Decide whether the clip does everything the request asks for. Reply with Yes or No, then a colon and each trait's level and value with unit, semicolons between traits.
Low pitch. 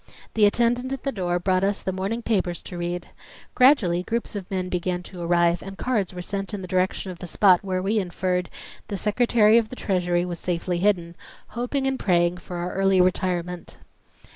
No: medium, 185 Hz